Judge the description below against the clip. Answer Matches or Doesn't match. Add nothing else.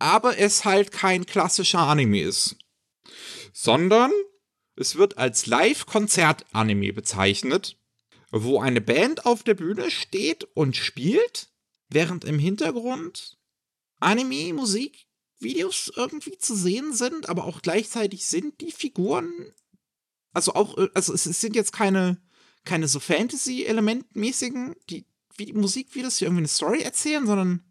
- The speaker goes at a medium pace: Doesn't match